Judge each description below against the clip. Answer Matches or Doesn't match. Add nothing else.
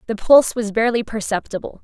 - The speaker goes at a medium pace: Matches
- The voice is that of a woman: Matches